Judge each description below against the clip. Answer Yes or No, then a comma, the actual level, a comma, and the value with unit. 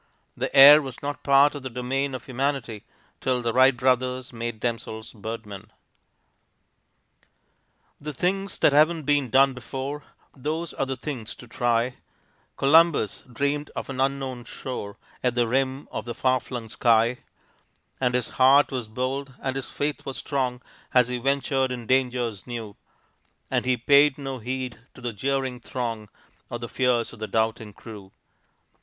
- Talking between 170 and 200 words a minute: No, average, 160 wpm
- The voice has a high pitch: No, low, 130 Hz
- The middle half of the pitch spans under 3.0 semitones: Yes, narrow, 2.5 semitones